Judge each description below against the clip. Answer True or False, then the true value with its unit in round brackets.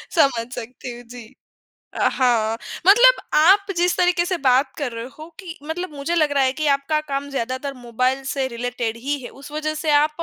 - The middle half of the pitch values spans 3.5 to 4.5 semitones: True (4.1 semitones)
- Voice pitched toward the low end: False (280 Hz)